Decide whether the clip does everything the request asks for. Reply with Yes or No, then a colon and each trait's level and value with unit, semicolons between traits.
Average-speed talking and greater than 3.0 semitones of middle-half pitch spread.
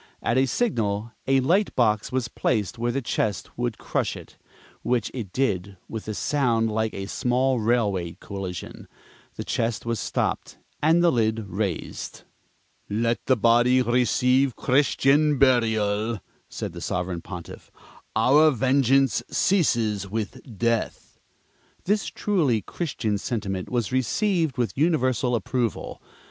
No: slow, 130 wpm; average, 3.8 semitones